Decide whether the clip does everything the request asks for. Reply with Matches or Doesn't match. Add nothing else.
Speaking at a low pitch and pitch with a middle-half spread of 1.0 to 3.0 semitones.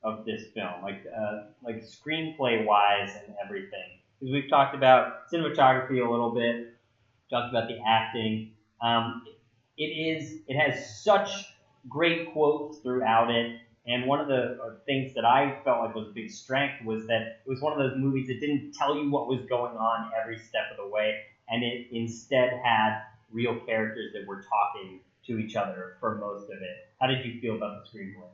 Doesn't match